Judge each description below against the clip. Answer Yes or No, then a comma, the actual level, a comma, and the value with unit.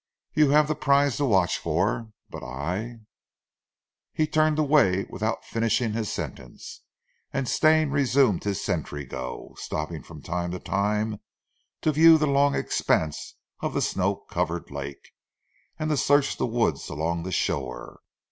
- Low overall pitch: Yes, low, 110 Hz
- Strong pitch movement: Yes, wide, 9.0 semitones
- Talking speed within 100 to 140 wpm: No, average, 150 wpm